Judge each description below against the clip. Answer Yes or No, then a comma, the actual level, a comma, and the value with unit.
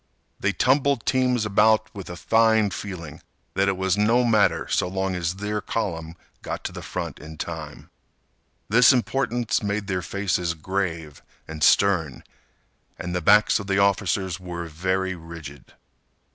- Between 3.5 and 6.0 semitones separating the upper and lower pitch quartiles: Yes, average, 3.9 semitones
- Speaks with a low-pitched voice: Yes, very low, 95 Hz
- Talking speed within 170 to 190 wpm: No, average, 150 wpm